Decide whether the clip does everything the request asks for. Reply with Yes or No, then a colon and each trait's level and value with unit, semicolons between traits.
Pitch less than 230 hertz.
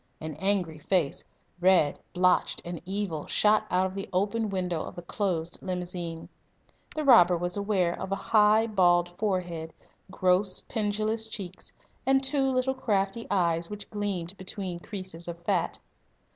Yes: high, 190 Hz